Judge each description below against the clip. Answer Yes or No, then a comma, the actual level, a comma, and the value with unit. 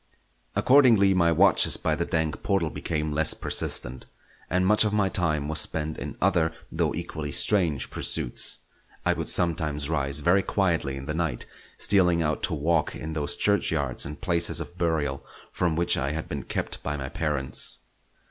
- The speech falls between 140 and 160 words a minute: No, average, 170 wpm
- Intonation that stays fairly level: No, average, 3.1 semitones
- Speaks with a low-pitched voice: Yes, very low, 80 Hz